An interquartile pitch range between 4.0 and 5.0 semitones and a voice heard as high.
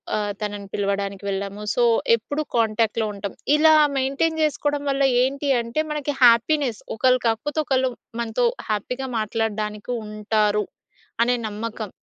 Yes: average, 4.3 semitones; high, 230 Hz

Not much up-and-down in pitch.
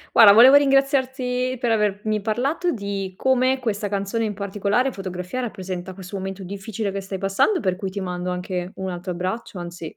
No: average, 4.3 semitones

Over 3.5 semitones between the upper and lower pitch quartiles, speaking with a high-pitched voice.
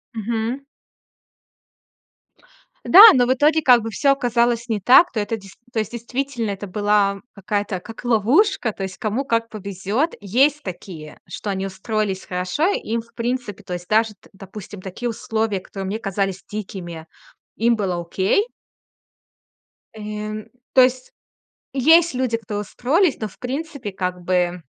Yes: average, 4.0 semitones; high, 215 Hz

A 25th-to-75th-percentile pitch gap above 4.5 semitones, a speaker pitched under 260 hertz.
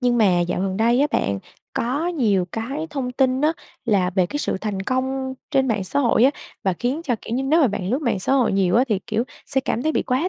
Yes: average, 5.1 semitones; high, 245 Hz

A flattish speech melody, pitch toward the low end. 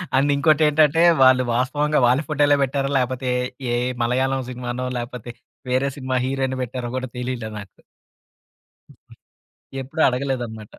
Yes: narrow, 2.1 semitones; low, 130 Hz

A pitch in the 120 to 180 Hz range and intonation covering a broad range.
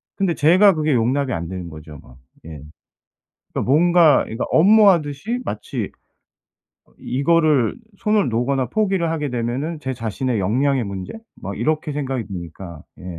Yes: low, 135 Hz; wide, 6.7 semitones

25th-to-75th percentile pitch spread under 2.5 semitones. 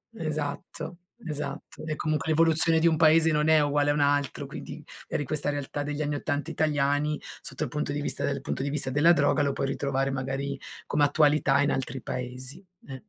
Yes: narrow, 1.7 semitones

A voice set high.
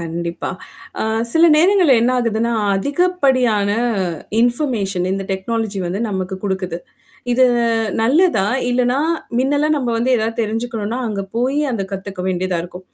Yes: high, 225 Hz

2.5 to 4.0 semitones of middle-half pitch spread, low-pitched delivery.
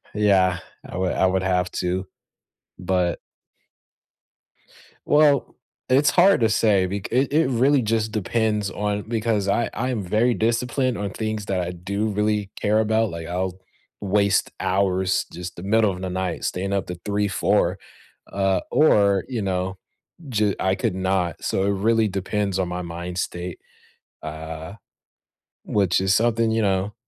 Yes: average, 3.0 semitones; low, 100 Hz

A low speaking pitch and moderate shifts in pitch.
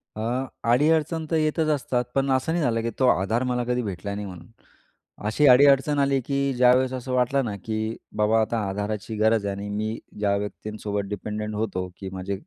Yes: low, 115 Hz; average, 4.3 semitones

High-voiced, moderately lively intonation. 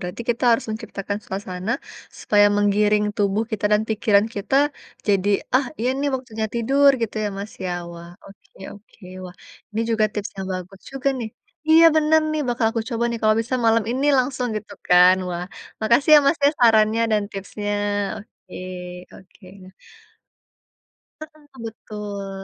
Yes: high, 215 Hz; average, 3.1 semitones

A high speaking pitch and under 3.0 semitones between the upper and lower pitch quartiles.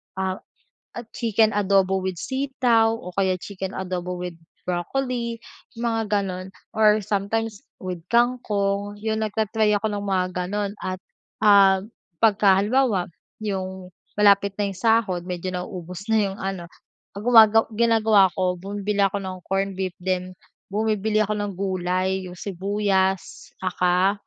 Yes: high, 200 Hz; narrow, 2.5 semitones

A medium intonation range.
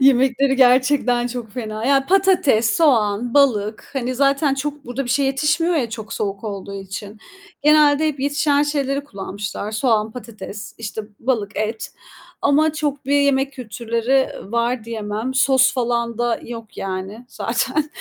Yes: average, 4.2 semitones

